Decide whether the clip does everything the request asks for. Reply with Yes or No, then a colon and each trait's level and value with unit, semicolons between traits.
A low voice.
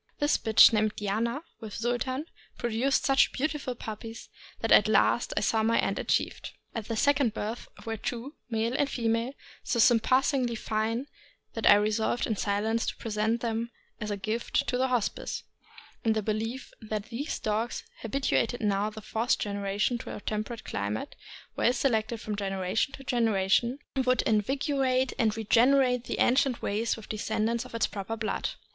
No: high, 225 Hz